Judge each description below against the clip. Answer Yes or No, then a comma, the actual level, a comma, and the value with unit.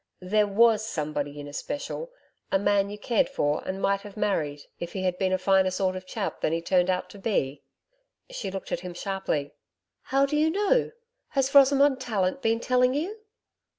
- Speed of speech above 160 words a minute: Yes, average, 190 wpm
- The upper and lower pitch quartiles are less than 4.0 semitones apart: No, wide, 5.6 semitones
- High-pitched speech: Yes, high, 200 Hz